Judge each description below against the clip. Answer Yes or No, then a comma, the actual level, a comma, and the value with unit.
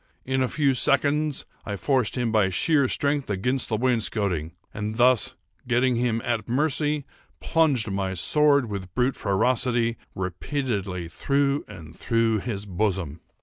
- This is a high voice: No, low, 120 Hz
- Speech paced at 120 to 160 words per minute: Yes, average, 140 wpm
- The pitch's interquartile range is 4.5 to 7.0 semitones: Yes, average, 5.2 semitones